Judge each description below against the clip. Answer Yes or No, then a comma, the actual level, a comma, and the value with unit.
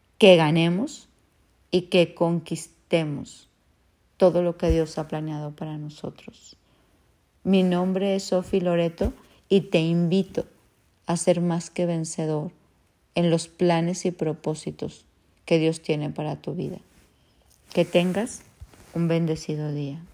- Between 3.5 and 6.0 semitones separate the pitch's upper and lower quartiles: No, narrow, 2.4 semitones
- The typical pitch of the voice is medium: Yes, medium, 170 Hz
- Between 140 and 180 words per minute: No, slow, 125 wpm